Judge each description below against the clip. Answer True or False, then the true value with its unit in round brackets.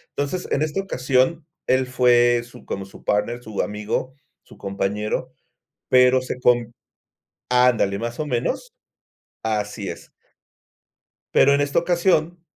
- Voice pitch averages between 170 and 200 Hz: False (125 Hz)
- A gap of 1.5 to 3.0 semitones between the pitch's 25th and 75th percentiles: False (4.3 semitones)